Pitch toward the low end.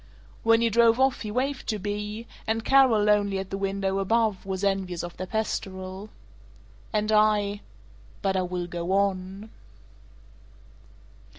No: high, 205 Hz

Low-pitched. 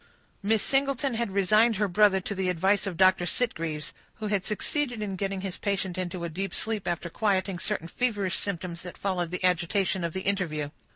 No: high, 190 Hz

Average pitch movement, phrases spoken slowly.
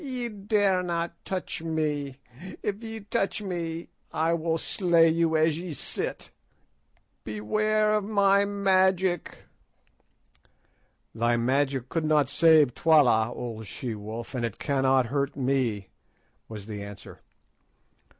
No: wide, 6.8 semitones; slow, 120 wpm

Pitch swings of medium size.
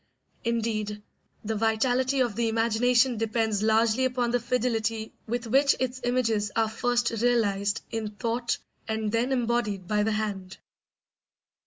No: narrow, 2.0 semitones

